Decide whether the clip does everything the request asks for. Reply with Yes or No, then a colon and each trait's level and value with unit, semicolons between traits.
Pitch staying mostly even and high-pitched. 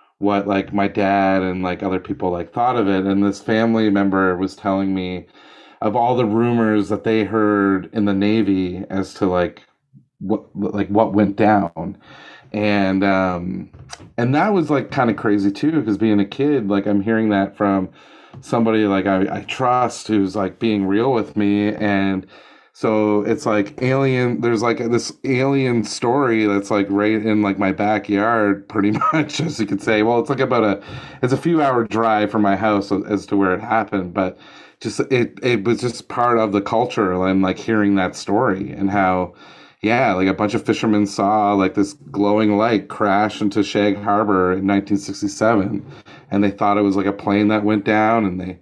No: narrow, 2.2 semitones; low, 105 Hz